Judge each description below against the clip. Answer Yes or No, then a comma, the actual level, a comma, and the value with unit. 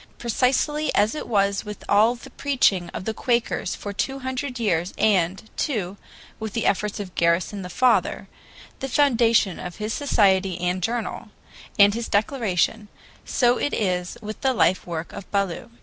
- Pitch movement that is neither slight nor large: Yes, average, 4.4 semitones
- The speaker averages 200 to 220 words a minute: No, average, 165 wpm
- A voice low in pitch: No, high, 210 Hz